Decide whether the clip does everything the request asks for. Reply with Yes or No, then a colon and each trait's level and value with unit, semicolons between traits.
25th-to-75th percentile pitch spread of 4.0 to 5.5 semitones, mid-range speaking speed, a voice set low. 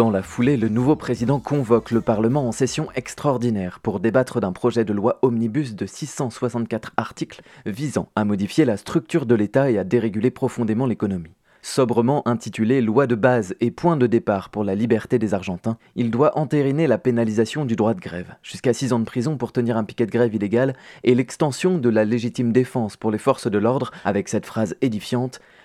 No: average, 2.9 semitones; average, 195 wpm; low, 120 Hz